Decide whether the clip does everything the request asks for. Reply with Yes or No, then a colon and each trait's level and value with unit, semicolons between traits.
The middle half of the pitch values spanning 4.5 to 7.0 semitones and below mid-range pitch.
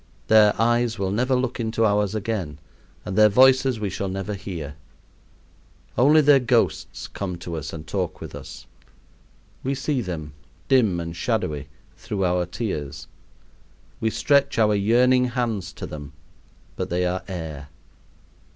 Yes: wide, 5.4 semitones; low, 105 Hz